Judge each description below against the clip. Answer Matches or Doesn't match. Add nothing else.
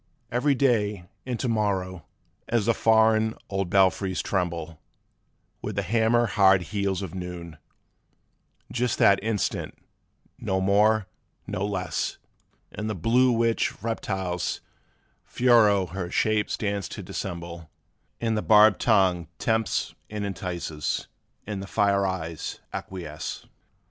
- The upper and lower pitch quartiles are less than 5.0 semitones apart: Matches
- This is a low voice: Matches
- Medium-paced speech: Doesn't match